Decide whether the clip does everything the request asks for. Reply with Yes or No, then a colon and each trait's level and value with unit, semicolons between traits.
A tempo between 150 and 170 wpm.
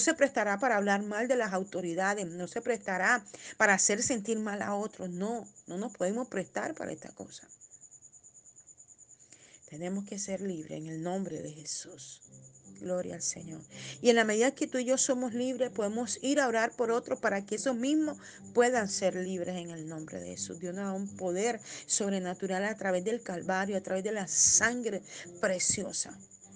No: average, 185 wpm